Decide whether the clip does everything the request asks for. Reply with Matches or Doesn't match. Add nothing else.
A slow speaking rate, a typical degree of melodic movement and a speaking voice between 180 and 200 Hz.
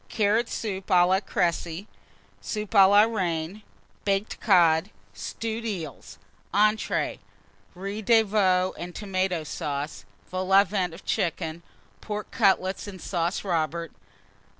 Matches